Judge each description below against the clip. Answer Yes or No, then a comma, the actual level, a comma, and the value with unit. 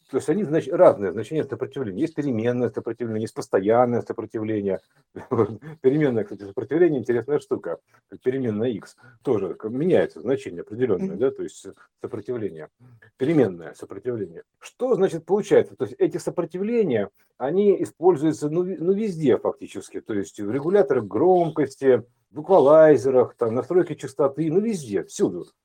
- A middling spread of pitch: No, wide, 8.8 semitones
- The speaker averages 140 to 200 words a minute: No, average, 125 wpm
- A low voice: No, medium, 160 Hz